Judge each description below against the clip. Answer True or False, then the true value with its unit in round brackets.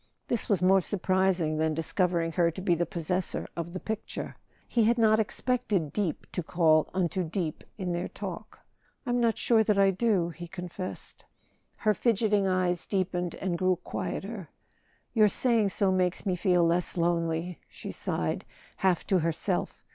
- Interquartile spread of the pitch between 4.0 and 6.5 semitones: False (3.1 semitones)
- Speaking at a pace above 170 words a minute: False (160 wpm)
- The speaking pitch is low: False (185 Hz)